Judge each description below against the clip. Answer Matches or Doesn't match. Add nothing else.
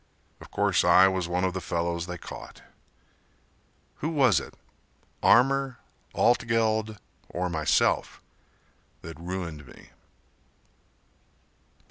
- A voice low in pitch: Matches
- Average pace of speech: Doesn't match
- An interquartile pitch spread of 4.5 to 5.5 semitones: Matches